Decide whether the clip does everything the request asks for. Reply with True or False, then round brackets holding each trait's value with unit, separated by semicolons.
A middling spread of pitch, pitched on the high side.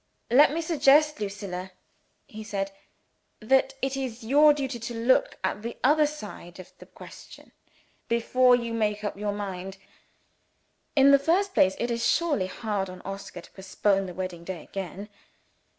False (5.7 semitones; 225 Hz)